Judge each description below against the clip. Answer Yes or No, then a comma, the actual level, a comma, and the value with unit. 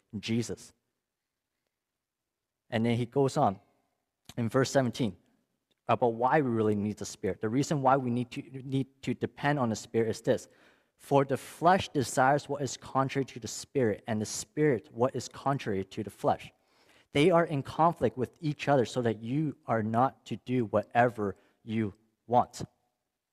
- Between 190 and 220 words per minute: No, average, 170 wpm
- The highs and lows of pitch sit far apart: No, average, 3.7 semitones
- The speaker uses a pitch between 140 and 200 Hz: No, low, 125 Hz